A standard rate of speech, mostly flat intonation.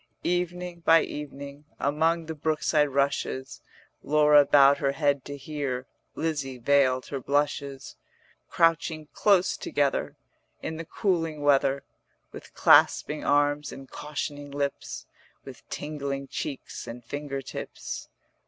No: slow, 115 wpm; narrow, 2.2 semitones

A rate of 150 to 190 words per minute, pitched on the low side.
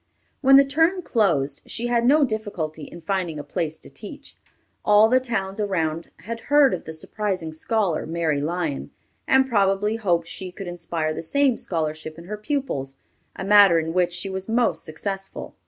No: average, 175 wpm; high, 190 Hz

